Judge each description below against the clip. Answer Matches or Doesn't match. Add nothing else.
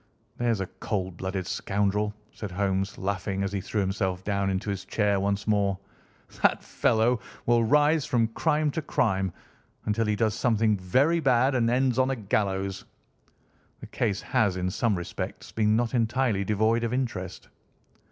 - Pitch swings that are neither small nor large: Matches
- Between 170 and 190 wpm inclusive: Doesn't match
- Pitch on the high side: Doesn't match